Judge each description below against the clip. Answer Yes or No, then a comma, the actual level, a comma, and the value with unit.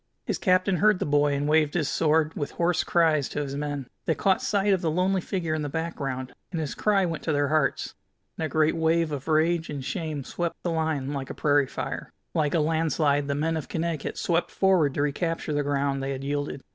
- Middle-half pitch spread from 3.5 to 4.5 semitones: No, average, 2.7 semitones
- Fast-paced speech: Yes, fast, 230 wpm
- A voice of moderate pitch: Yes, medium, 155 Hz